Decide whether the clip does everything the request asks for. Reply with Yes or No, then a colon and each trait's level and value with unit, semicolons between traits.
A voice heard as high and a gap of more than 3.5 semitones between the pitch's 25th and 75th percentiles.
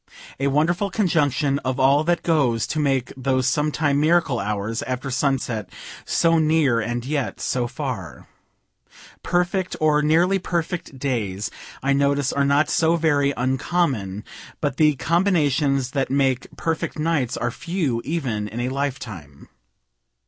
No: medium, 140 Hz; average, 4.0 semitones